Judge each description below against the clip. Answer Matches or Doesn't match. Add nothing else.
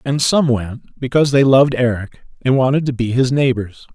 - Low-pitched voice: Matches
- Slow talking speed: Doesn't match